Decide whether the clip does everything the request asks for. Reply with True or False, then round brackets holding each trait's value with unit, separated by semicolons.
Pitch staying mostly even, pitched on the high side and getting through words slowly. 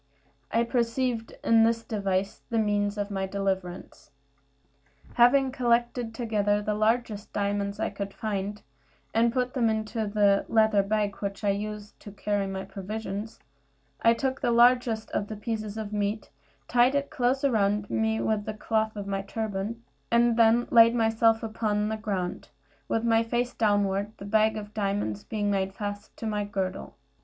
False (2.1 semitones; 215 Hz; 165 wpm)